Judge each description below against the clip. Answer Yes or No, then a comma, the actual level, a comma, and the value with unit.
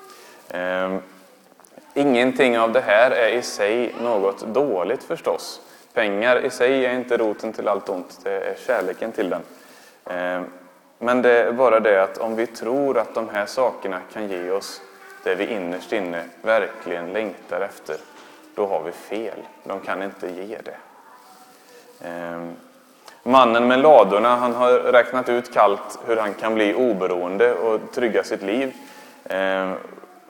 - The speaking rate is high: No, average, 155 wpm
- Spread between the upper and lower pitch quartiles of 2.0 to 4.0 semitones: No, average, 5.2 semitones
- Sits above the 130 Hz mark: No, low, 120 Hz